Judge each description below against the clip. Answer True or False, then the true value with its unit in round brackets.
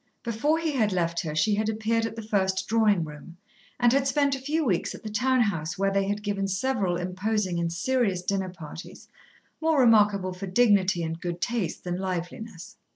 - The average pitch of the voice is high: True (200 Hz)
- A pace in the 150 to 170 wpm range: False (195 wpm)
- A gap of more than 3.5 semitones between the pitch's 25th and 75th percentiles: True (4.1 semitones)